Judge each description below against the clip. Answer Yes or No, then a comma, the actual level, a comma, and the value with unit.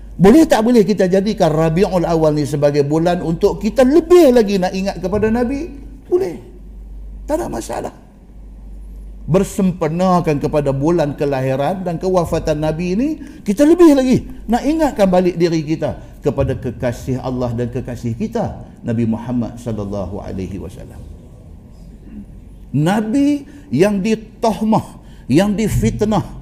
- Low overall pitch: No, medium, 175 Hz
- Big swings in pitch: Yes, wide, 8.6 semitones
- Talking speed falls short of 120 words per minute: No, average, 125 wpm